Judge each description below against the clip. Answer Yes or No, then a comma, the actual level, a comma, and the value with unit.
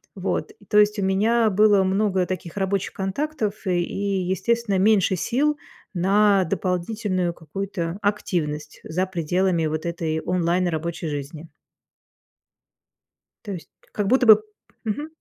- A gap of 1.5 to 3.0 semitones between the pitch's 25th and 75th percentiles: No, average, 3.4 semitones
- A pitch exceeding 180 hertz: Yes, high, 190 Hz